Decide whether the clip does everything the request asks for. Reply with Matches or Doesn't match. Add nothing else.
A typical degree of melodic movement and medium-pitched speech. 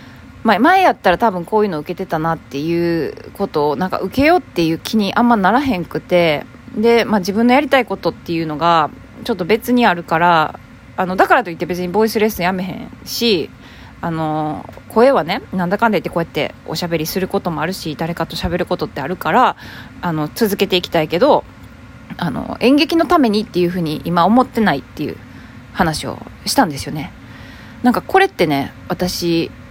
Doesn't match